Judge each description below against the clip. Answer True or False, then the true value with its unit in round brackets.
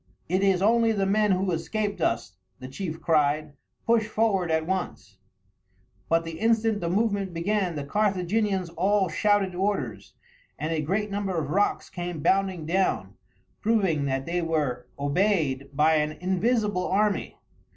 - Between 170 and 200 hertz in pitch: True (185 Hz)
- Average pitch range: True (4.6 semitones)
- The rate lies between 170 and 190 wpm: False (150 wpm)